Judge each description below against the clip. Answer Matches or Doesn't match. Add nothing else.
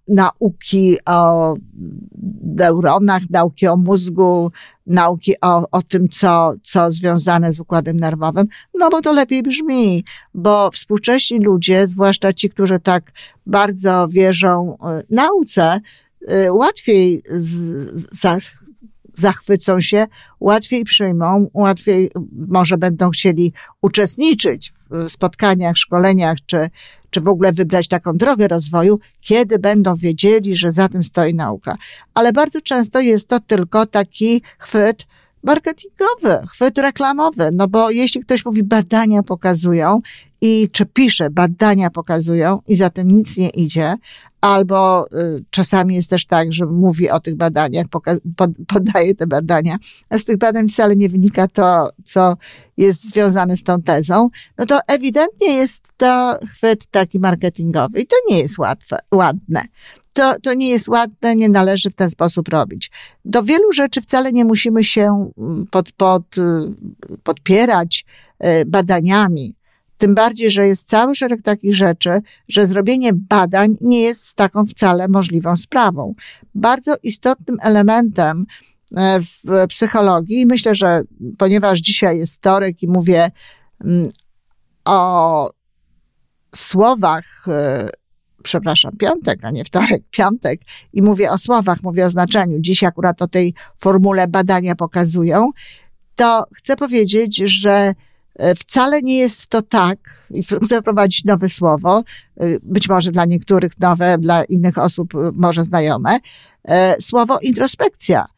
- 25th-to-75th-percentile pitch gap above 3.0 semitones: Matches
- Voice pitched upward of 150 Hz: Matches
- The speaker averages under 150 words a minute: Matches